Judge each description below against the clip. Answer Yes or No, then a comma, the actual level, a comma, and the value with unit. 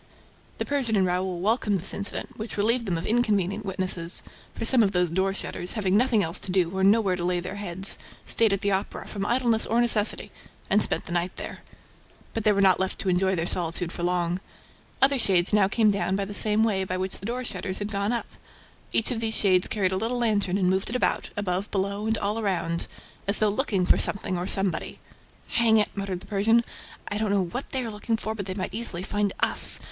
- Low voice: No, high, 200 Hz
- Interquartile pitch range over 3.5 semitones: No, average, 3.0 semitones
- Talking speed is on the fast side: Yes, fast, 230 wpm